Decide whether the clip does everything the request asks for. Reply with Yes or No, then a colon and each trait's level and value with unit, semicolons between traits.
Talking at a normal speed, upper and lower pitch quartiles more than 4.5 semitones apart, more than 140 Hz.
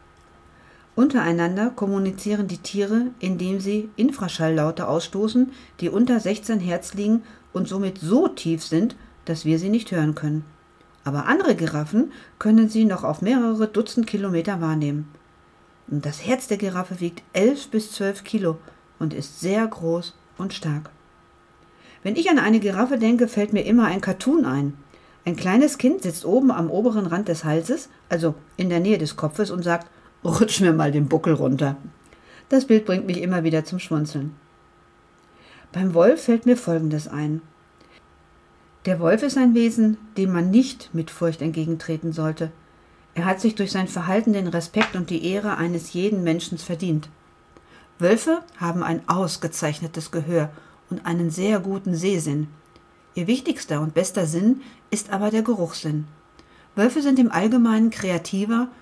Yes: average, 155 wpm; average, 5.2 semitones; medium, 185 Hz